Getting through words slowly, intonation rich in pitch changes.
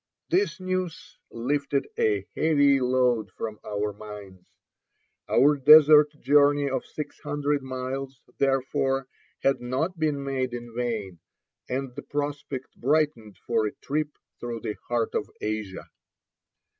No: slow, 125 wpm; average, 4.0 semitones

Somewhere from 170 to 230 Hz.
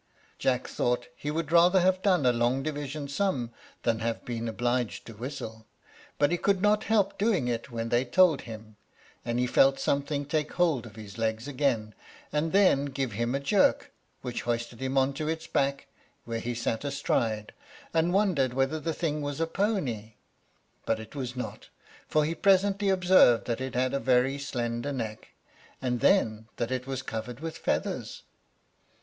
No: low, 135 Hz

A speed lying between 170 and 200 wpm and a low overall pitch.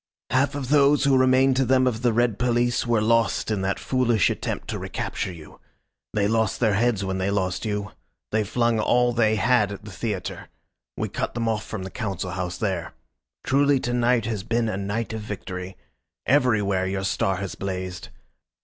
Yes: average, 190 wpm; low, 110 Hz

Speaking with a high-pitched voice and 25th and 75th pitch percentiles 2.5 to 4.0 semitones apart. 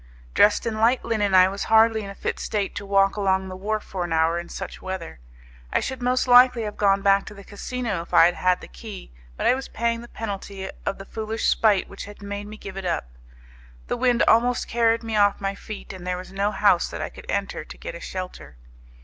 Yes: high, 205 Hz; average, 3.0 semitones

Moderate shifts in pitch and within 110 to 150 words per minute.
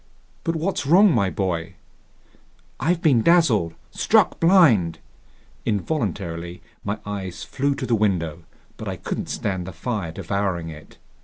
No: wide, 8.4 semitones; slow, 135 wpm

